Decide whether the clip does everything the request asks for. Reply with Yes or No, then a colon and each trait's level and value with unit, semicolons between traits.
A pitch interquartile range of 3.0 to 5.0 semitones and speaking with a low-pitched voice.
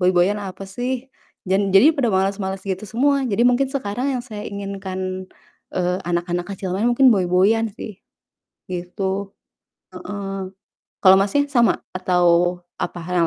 No: average, 3.6 semitones; high, 195 Hz